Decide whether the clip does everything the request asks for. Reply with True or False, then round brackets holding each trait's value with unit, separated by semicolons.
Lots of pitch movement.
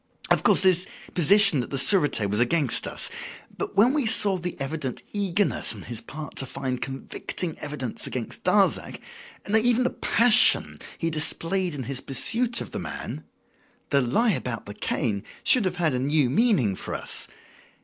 True (7.6 semitones)